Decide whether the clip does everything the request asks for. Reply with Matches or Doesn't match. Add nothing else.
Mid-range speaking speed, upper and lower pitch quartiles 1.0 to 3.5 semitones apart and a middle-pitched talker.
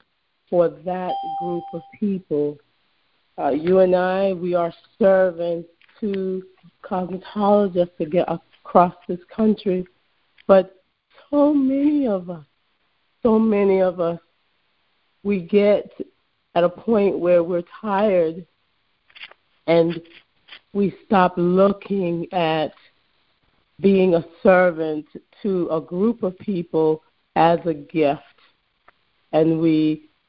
Doesn't match